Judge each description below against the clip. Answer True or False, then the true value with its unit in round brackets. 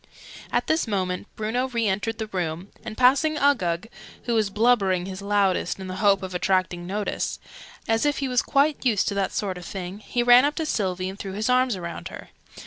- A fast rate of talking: True (210 wpm)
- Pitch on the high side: True (205 Hz)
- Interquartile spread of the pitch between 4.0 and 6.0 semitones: True (4.6 semitones)